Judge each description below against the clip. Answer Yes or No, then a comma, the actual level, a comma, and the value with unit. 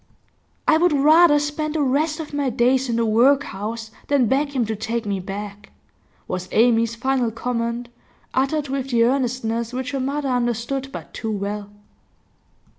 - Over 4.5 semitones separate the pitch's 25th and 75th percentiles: No, average, 3.6 semitones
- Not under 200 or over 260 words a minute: No, average, 160 wpm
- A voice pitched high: Yes, very high, 250 Hz